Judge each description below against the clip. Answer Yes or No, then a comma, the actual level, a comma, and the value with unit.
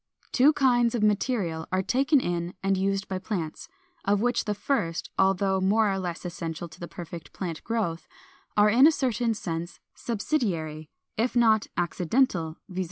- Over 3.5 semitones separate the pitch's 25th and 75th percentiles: Yes, average, 5.2 semitones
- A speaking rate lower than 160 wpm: No, average, 165 wpm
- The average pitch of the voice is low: No, high, 195 Hz